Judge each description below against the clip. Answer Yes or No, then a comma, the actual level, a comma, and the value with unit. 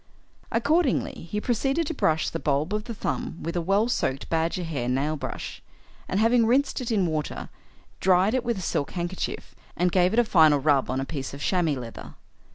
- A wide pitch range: Yes, wide, 6.9 semitones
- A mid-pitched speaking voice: Yes, medium, 180 Hz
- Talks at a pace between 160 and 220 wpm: Yes, average, 200 wpm